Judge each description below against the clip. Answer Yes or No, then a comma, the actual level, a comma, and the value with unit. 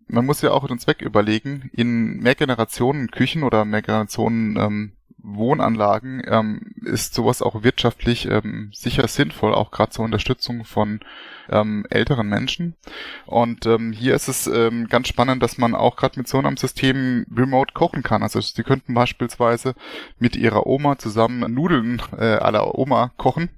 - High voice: No, low, 120 Hz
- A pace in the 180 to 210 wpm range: No, average, 160 wpm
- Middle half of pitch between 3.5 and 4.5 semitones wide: No, average, 2.8 semitones